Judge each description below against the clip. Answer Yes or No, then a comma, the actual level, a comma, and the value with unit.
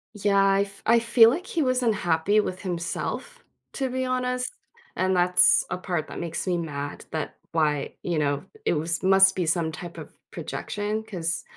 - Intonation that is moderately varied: Yes, average, 4.8 semitones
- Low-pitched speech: No, medium, 185 Hz